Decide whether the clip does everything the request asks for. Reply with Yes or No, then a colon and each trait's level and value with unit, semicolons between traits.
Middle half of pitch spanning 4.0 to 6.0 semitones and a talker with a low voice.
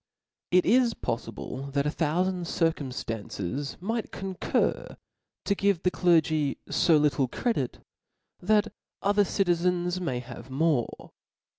No: average, 5.2 semitones; medium, 165 Hz